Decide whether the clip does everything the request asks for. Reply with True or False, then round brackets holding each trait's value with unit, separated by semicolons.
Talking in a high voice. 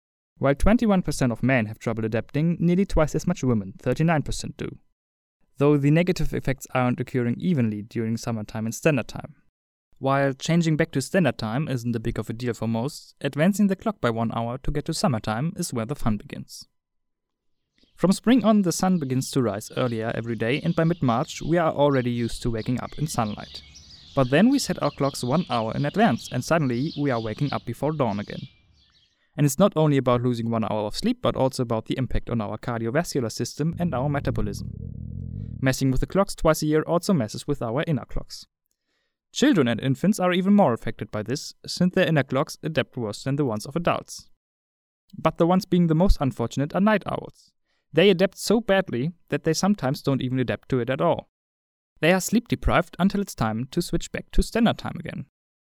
False (135 Hz)